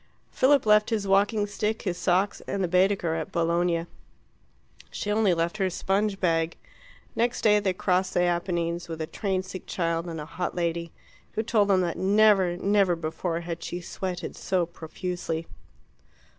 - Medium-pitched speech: Yes, medium, 180 Hz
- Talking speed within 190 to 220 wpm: No, average, 165 wpm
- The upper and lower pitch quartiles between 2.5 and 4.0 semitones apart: Yes, average, 3.0 semitones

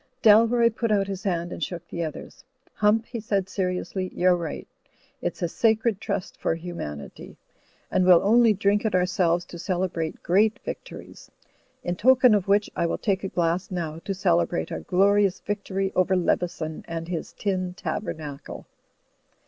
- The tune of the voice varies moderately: Yes, average, 3.1 semitones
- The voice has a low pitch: No, medium, 185 Hz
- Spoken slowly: No, average, 165 wpm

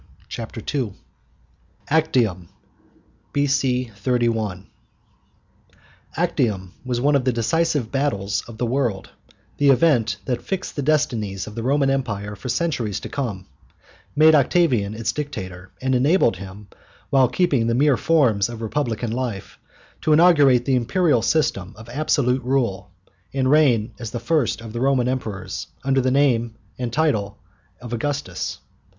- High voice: No, low, 125 Hz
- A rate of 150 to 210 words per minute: No, average, 140 wpm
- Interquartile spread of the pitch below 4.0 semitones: No, average, 4.4 semitones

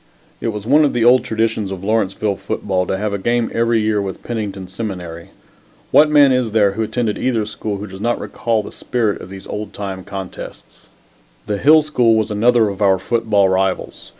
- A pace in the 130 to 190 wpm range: No, average, 200 wpm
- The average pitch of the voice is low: Yes, low, 105 Hz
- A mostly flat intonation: No, average, 3.1 semitones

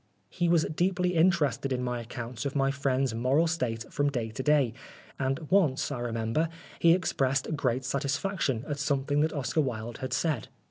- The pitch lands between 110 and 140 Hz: Yes, low, 135 Hz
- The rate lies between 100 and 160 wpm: No, average, 175 wpm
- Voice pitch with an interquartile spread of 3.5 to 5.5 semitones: Yes, average, 3.8 semitones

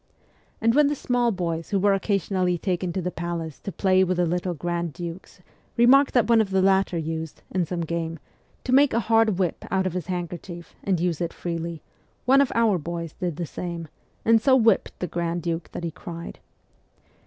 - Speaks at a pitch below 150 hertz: No, medium, 180 Hz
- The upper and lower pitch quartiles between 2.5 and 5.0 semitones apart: Yes, average, 3.3 semitones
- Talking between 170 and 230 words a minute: Yes, average, 200 wpm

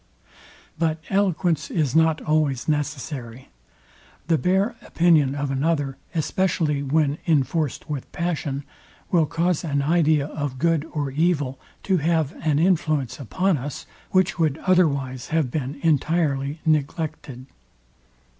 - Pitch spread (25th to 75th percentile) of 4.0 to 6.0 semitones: No, average, 3.0 semitones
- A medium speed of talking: No, slow, 120 wpm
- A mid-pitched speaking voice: Yes, medium, 155 Hz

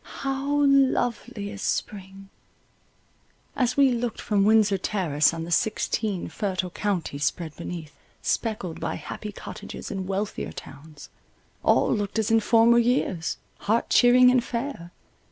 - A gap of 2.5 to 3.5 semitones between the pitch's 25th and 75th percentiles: No, average, 4.7 semitones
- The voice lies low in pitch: No, high, 210 Hz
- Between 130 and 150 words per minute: Yes, slow, 135 wpm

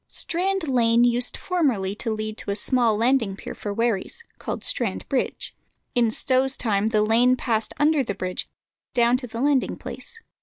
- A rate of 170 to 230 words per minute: Yes, average, 175 wpm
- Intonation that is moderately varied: Yes, average, 3.4 semitones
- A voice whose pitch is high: Yes, high, 235 Hz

